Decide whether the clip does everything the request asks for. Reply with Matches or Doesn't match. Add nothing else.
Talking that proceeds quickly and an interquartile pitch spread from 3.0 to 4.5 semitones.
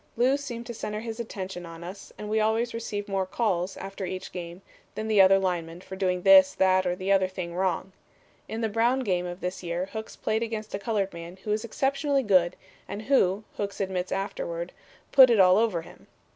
Matches